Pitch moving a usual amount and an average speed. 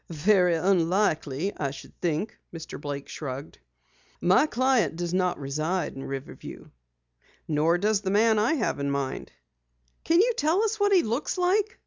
No: wide, 7.5 semitones; average, 150 wpm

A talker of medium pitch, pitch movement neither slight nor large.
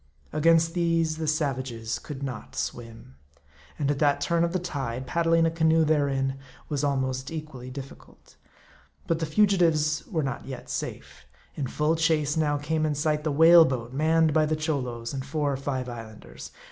Yes: medium, 150 Hz; average, 3.3 semitones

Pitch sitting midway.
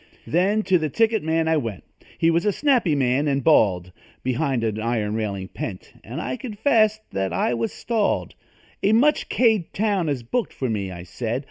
Yes: medium, 150 Hz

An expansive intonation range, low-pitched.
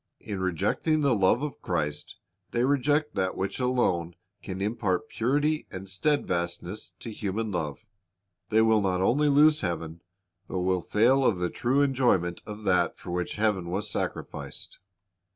Yes: wide, 5.8 semitones; low, 105 Hz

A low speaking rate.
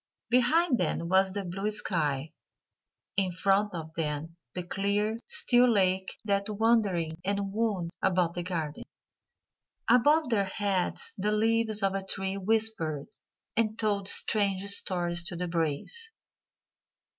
Yes: slow, 130 wpm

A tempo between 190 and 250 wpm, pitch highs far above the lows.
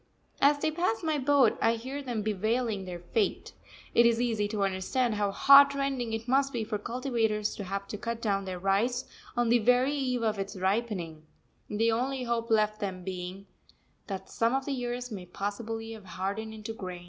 No: average, 195 wpm; average, 3.8 semitones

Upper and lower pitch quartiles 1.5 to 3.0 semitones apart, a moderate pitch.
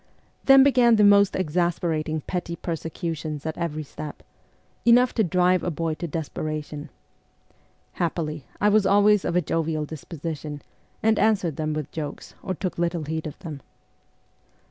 No: average, 3.5 semitones; medium, 165 Hz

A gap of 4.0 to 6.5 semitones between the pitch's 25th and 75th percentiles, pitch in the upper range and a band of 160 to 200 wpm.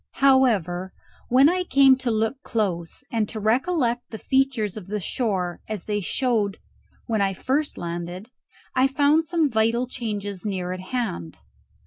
No: average, 5.2 semitones; high, 220 Hz; average, 150 wpm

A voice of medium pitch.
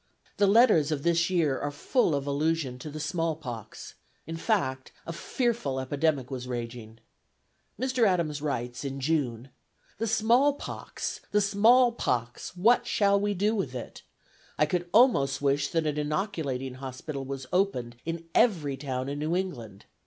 Yes: medium, 155 Hz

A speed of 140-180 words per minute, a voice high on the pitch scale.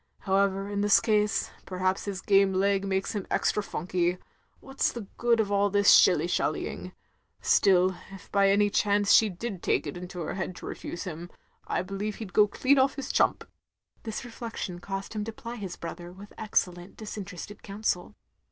No: average, 190 wpm; high, 200 Hz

